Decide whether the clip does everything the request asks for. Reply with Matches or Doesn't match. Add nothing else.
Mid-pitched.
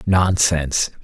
Doesn't match